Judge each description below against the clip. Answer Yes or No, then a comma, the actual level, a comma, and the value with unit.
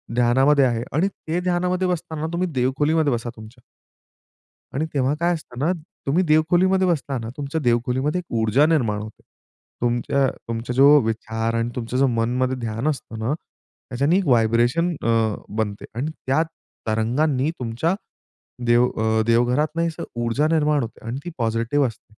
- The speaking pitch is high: No, low, 130 Hz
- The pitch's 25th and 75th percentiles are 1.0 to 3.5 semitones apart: No, average, 5.0 semitones